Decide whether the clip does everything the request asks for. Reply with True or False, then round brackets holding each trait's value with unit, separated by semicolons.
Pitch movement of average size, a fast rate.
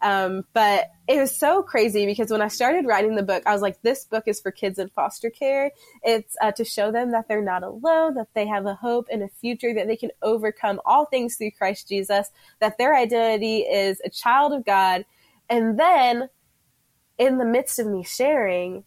True (3.2 semitones; 210 wpm)